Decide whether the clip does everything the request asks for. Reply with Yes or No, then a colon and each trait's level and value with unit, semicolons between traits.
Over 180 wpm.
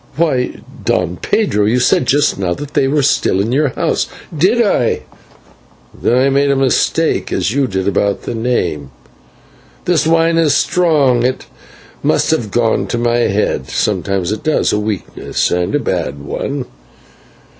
No: average, 160 wpm